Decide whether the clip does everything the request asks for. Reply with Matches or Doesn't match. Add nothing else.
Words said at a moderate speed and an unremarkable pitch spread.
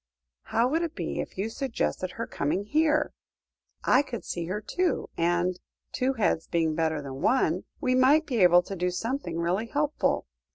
Doesn't match